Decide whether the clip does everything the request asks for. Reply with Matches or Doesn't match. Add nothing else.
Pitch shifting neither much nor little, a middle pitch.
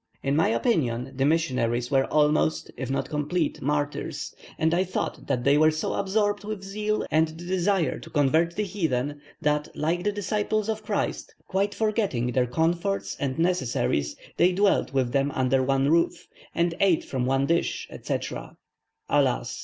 Doesn't match